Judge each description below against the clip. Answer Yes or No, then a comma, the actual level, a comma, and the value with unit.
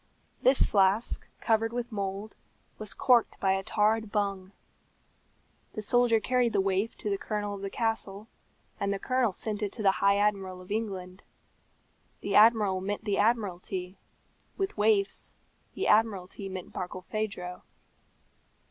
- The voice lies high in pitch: Yes, high, 205 Hz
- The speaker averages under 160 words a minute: Yes, average, 140 wpm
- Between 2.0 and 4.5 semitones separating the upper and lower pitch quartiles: Yes, narrow, 2.4 semitones